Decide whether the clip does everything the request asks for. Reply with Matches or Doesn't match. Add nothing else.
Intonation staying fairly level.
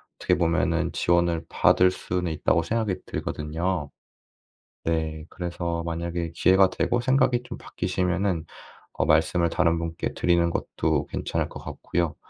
Matches